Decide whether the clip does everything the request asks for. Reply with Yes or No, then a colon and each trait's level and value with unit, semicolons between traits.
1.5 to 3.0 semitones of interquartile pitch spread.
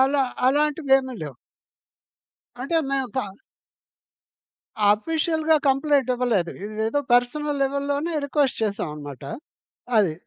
No: average, 5.0 semitones